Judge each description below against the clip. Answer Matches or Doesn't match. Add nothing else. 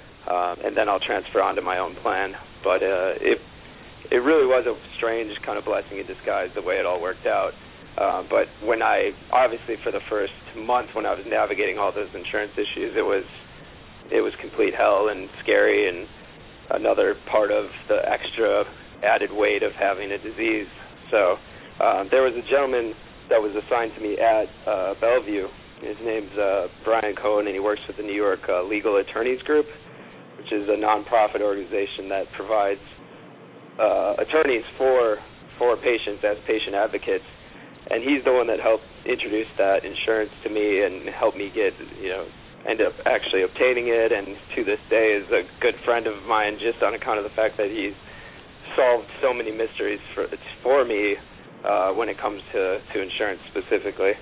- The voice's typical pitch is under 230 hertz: Doesn't match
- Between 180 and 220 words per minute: Matches